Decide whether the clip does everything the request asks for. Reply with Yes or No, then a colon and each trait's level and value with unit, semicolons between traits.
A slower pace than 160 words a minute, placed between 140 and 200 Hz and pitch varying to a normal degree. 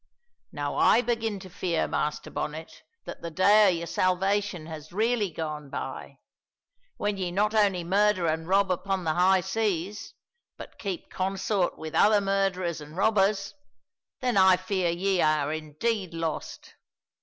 Yes: average, 150 wpm; medium, 185 Hz; average, 3.4 semitones